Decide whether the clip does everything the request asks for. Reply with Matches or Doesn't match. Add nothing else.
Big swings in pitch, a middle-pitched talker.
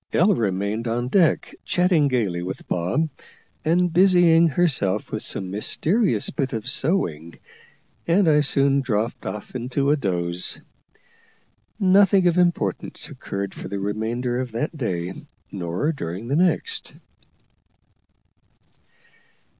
Doesn't match